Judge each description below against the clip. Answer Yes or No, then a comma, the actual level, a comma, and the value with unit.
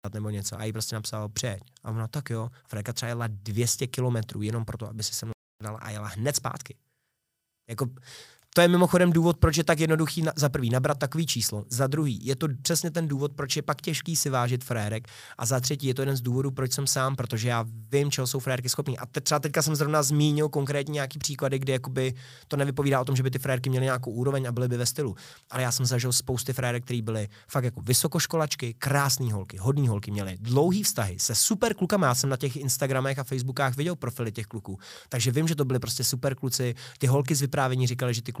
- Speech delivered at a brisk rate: Yes, fast, 230 wpm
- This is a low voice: Yes, low, 130 Hz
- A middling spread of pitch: Yes, average, 3.3 semitones